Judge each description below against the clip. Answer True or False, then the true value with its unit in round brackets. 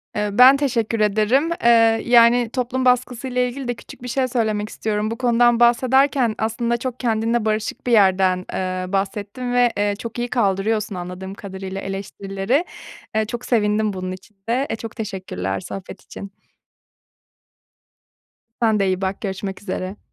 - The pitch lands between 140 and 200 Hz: False (220 Hz)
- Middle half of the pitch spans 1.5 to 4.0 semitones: True (3.7 semitones)